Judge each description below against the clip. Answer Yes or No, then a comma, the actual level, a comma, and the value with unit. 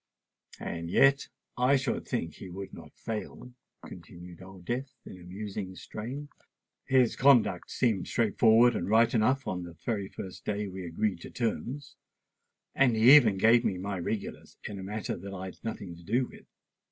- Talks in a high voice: No, low, 105 Hz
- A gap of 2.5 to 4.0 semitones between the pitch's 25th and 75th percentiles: No, average, 4.5 semitones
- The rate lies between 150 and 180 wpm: Yes, average, 170 wpm